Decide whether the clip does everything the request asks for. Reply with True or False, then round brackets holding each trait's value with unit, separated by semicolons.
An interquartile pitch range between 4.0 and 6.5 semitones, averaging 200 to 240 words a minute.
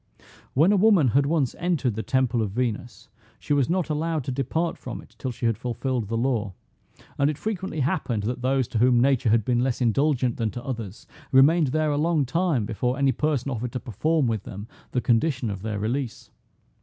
True (4.5 semitones; 205 wpm)